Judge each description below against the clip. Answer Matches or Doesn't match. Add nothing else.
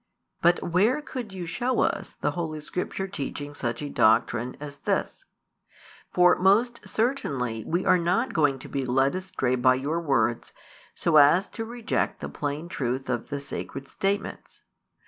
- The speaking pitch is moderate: Matches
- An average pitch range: Doesn't match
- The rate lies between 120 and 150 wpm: Doesn't match